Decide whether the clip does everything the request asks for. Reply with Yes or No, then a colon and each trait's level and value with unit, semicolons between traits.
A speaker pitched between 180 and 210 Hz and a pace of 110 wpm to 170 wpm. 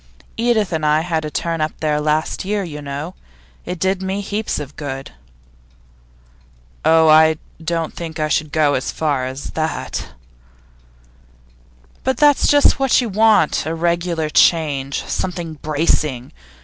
No: medium, 160 Hz; average, 145 wpm